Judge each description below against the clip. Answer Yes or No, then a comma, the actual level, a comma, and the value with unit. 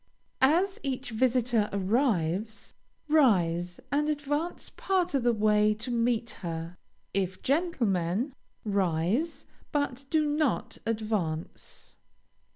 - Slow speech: Yes, slow, 100 wpm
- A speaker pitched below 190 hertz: No, high, 230 Hz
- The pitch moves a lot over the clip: Yes, wide, 6.6 semitones